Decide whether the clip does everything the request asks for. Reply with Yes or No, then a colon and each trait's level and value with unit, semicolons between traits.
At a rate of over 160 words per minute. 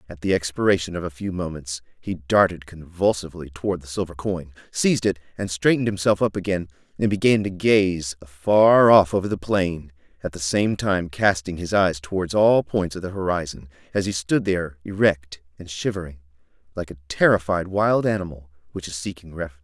Yes: average, 180 wpm